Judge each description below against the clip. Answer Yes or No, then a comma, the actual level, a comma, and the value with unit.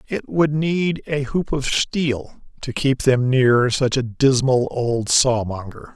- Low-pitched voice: Yes, low, 130 Hz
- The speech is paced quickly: No, average, 160 wpm